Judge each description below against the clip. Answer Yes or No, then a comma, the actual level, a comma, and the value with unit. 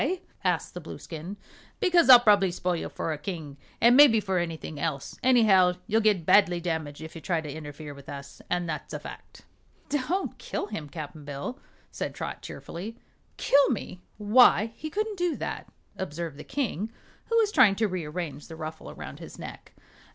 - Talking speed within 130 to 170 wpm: No, average, 180 wpm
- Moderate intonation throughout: No, wide, 6.7 semitones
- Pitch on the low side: No, medium, 180 Hz